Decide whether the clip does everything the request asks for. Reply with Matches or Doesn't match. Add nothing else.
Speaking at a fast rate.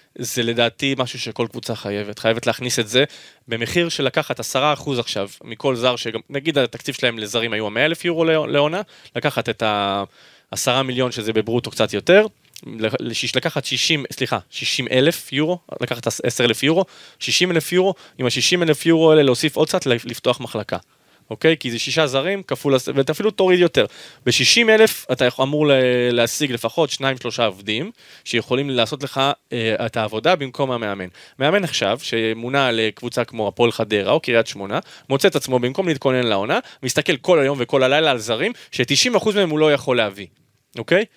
Matches